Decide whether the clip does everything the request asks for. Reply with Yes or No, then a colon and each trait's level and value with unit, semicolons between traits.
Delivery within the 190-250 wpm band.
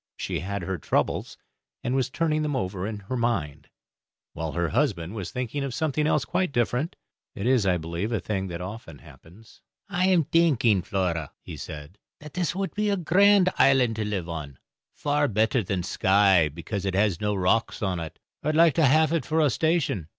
Yes: average, 200 wpm